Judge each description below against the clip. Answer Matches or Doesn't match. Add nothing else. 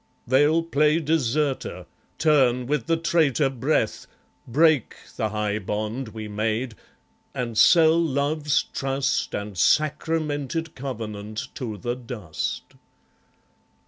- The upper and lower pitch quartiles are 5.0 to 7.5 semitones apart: Matches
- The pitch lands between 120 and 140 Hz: Matches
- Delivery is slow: Matches